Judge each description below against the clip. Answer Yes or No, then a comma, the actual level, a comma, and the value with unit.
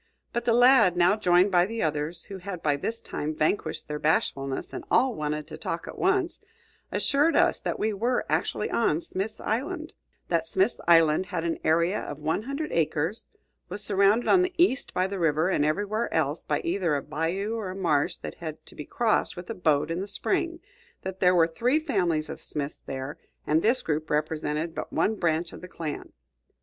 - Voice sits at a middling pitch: Yes, medium, 180 Hz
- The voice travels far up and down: Yes, wide, 5.9 semitones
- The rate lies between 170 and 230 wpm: Yes, average, 200 wpm